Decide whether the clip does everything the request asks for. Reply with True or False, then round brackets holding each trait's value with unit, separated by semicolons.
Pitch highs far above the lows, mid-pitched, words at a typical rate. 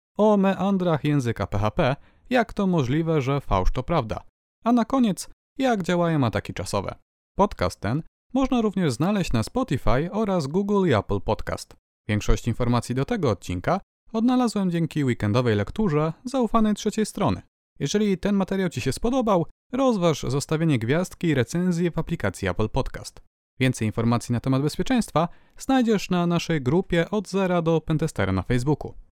True (8.3 semitones; 160 Hz; 150 wpm)